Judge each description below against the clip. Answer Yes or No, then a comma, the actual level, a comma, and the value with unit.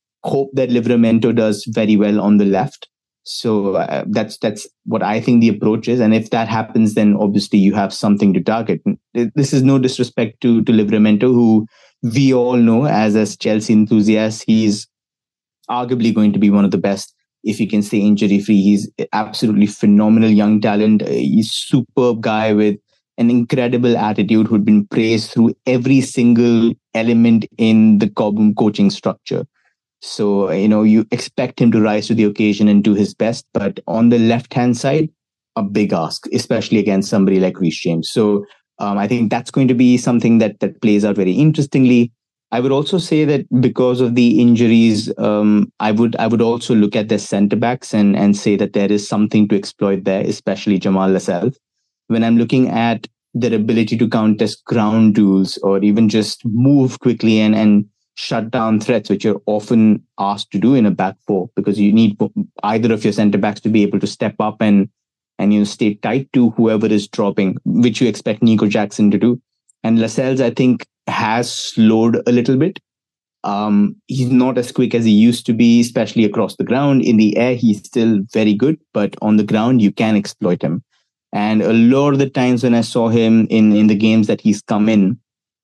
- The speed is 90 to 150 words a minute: No, average, 195 wpm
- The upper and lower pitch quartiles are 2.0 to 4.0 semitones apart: Yes, narrow, 2.5 semitones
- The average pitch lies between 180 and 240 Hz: No, low, 110 Hz